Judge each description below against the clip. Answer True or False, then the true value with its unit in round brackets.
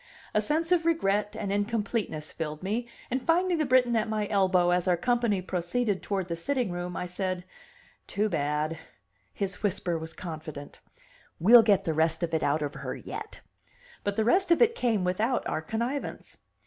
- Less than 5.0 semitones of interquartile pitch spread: False (5.5 semitones)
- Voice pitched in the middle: False (200 Hz)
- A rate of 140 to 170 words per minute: False (180 wpm)